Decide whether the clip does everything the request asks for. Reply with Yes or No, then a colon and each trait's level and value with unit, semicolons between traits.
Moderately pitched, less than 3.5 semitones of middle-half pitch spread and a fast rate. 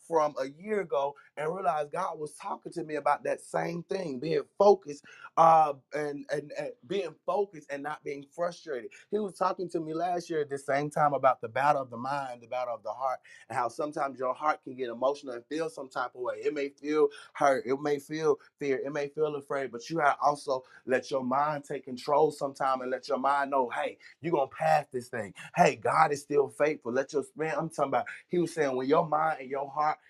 Yes: medium, 145 Hz; average, 2.8 semitones; fast, 235 wpm